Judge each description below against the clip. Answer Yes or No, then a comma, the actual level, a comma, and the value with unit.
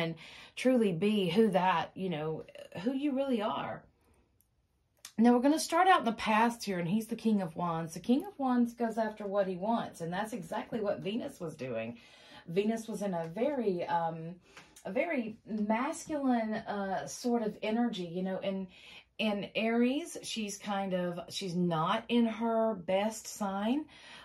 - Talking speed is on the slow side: No, average, 170 wpm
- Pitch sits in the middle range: No, high, 215 Hz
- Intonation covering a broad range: No, average, 4.1 semitones